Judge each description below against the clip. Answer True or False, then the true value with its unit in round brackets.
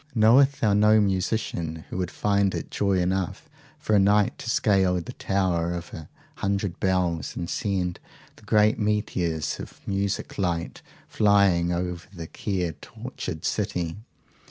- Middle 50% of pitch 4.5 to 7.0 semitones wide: False (2.9 semitones)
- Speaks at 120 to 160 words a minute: True (145 wpm)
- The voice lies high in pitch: False (95 Hz)